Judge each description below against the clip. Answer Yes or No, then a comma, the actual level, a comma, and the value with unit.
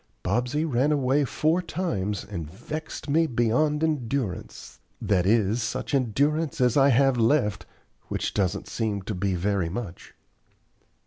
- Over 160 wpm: No, slow, 135 wpm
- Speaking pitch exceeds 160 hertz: No, low, 120 Hz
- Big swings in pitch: Yes, wide, 6.3 semitones